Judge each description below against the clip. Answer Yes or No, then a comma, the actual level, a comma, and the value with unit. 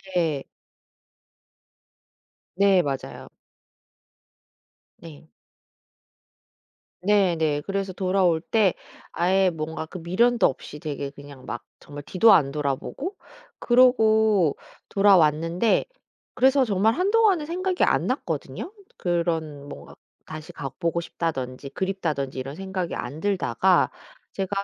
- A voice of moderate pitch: Yes, medium, 175 Hz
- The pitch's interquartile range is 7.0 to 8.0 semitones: No, average, 5.3 semitones